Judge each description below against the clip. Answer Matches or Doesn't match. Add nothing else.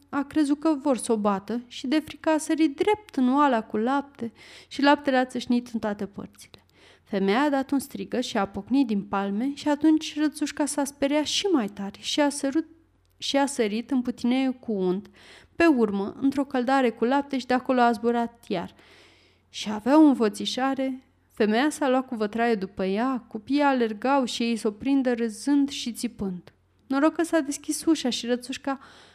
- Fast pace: Matches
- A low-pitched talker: Doesn't match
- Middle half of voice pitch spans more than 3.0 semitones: Matches